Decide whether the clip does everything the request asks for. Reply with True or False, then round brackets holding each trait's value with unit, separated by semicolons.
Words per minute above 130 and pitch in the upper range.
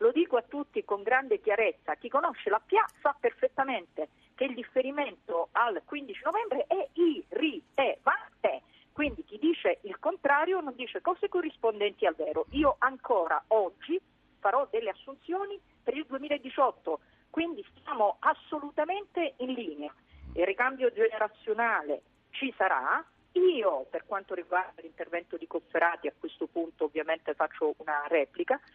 True (145 wpm; 260 Hz)